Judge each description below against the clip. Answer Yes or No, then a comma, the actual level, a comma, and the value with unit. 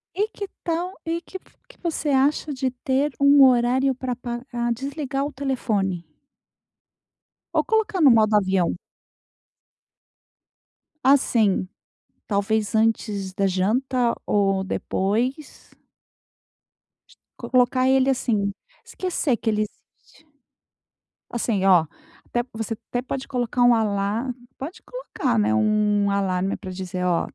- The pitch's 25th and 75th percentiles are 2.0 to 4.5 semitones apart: No, average, 5.1 semitones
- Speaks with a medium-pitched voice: No, high, 240 Hz